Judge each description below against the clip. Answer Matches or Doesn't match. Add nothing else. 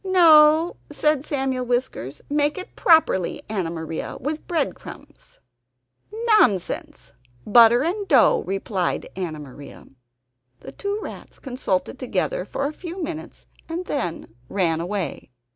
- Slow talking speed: Matches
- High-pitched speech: Matches